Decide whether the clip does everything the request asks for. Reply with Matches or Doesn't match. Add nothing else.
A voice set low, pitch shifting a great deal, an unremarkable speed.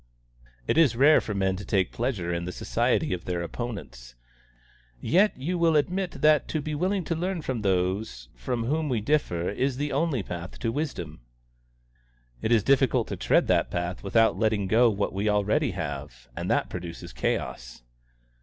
Matches